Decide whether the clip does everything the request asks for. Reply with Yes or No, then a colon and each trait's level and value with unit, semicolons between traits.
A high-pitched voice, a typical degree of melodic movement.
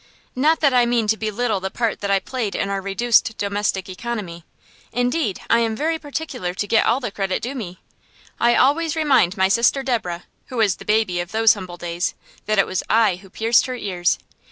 Yes: high, 220 Hz; average, 4.3 semitones